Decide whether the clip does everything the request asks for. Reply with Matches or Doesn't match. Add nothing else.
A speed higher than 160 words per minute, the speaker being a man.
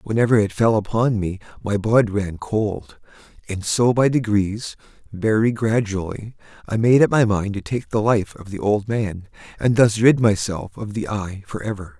Matches